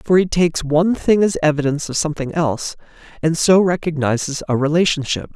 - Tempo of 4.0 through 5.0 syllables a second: No, 6.2 syllables/s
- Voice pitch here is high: No, medium, 160 Hz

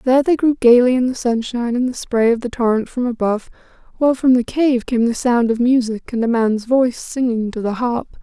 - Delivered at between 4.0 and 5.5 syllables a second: No, 5.7 syllables/s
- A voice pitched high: Yes, high, 240 Hz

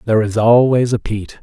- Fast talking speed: Yes, fast, 210 wpm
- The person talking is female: No, male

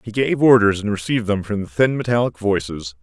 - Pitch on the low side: Yes, low, 105 Hz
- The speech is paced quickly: Yes, fast, 220 wpm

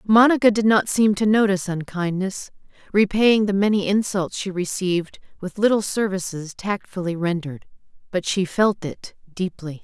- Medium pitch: No, high, 195 Hz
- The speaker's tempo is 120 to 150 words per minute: Yes, average, 140 wpm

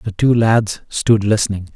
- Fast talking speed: No, average, 170 wpm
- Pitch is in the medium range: No, low, 105 Hz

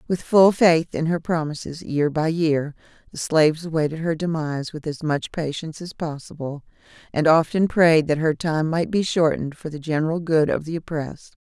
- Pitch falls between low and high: Yes, medium, 160 Hz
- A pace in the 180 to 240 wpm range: Yes, average, 190 wpm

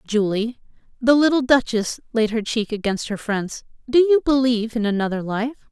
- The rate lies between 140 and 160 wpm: Yes, average, 145 wpm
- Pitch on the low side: No, high, 235 Hz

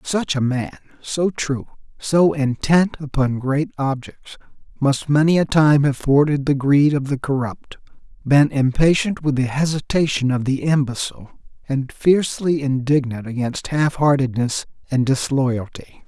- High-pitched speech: No, medium, 140 Hz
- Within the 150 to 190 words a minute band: No, average, 140 wpm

